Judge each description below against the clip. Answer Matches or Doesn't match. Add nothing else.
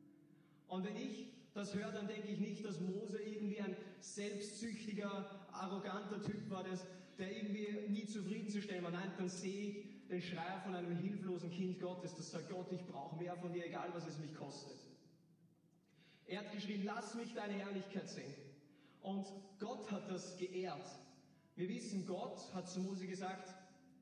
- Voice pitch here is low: Doesn't match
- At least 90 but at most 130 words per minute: Doesn't match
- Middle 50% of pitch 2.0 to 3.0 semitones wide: Matches